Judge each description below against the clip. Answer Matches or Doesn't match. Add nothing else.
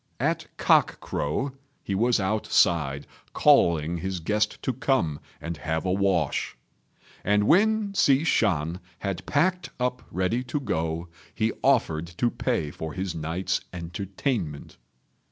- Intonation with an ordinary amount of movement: Doesn't match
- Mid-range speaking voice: Doesn't match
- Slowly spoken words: Matches